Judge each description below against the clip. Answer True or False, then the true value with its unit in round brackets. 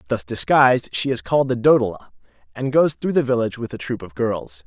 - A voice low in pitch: True (120 Hz)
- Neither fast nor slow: False (220 wpm)